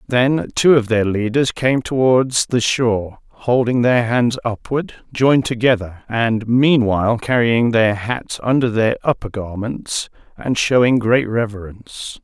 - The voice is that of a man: Yes, male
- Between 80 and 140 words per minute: Yes, slow, 135 wpm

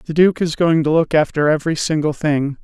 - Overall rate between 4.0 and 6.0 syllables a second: Yes, 5.5 syllables/s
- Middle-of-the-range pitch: Yes, medium, 155 Hz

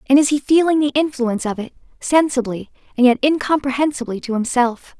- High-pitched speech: Yes, very high, 265 Hz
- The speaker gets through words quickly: No, average, 170 wpm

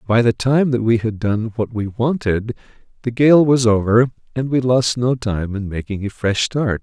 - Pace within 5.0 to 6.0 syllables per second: No, 4.6 syllables/s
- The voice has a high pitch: No, low, 115 Hz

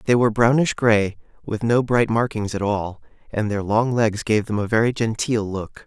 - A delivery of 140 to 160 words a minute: No, fast, 205 wpm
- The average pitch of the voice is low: Yes, low, 110 Hz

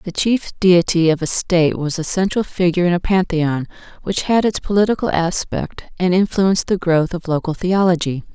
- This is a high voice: No, medium, 180 Hz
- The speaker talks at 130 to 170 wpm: No, average, 180 wpm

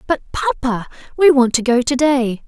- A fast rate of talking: No, average, 195 wpm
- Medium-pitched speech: No, very high, 265 Hz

